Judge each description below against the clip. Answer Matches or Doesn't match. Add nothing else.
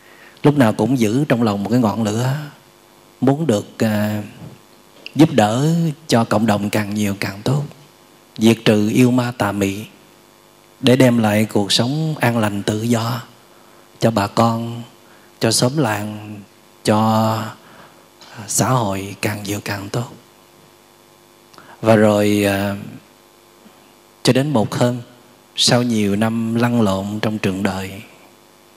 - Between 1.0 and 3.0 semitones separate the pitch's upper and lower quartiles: Matches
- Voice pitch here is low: Matches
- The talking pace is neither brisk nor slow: Doesn't match